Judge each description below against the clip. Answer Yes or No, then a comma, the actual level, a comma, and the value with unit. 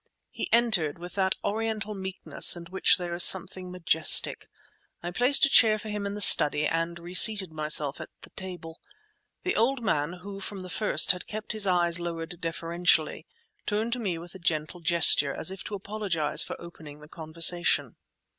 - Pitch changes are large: No, average, 3.7 semitones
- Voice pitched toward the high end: No, medium, 180 Hz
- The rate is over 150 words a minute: Yes, average, 180 wpm